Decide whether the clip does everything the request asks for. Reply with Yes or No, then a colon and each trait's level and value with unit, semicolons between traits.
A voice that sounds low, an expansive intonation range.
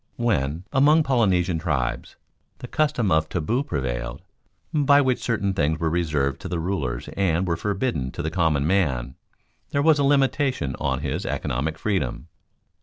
Yes: very low, 90 Hz; wide, 8.5 semitones